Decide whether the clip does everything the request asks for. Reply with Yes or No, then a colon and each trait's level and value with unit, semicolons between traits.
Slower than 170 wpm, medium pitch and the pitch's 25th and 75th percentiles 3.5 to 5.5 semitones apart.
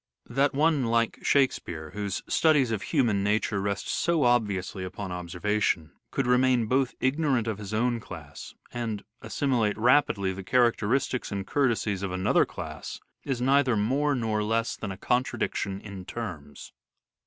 No: average, 155 wpm; low, 115 Hz; average, 4.5 semitones